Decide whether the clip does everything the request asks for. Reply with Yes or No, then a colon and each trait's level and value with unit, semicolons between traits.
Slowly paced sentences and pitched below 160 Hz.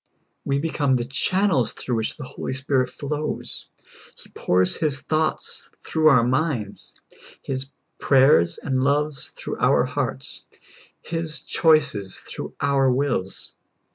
Yes: slow, 125 wpm; low, 135 Hz